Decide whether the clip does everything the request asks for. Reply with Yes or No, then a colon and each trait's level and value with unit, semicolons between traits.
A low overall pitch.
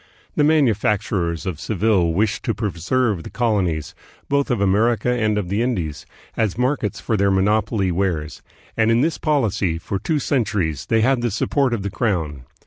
Yes: low, 105 Hz